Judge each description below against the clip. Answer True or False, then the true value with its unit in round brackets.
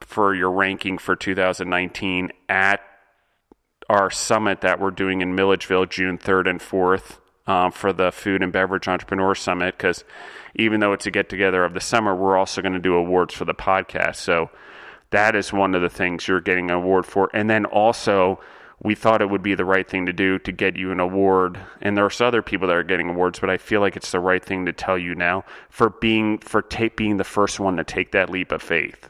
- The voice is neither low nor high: False (95 Hz)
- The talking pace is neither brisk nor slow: False (225 wpm)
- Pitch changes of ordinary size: False (1.5 semitones)